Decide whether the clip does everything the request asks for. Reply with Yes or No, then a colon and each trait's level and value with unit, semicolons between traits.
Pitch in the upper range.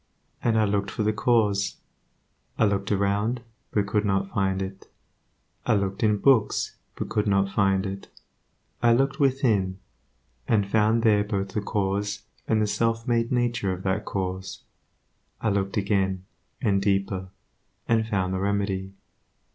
No: low, 100 Hz